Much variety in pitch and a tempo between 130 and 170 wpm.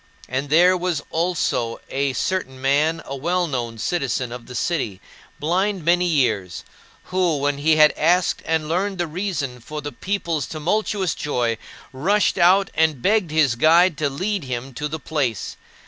No: average, 4.9 semitones; average, 165 wpm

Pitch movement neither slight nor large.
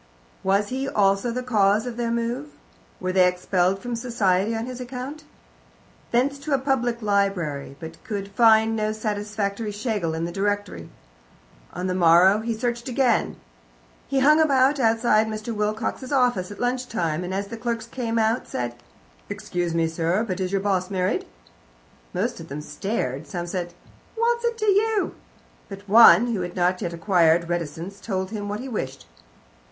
Yes: average, 4.7 semitones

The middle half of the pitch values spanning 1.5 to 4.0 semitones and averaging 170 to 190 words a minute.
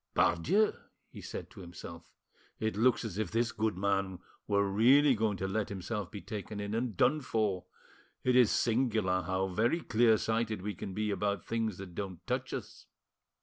Yes: average, 3.0 semitones; average, 180 wpm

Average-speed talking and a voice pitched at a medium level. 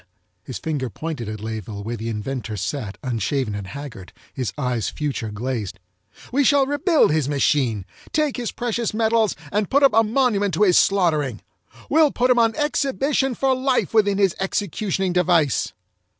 Yes: average, 165 wpm; medium, 175 Hz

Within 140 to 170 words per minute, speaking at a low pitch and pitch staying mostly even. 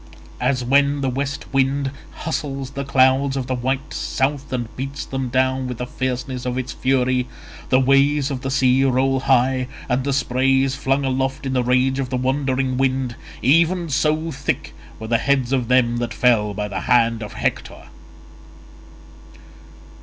Yes: average, 165 wpm; low, 130 Hz; narrow, 1.4 semitones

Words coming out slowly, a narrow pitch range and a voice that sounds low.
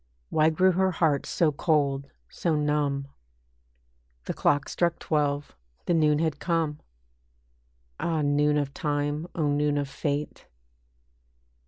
No: slow, 125 wpm; narrow, 1.8 semitones; medium, 150 Hz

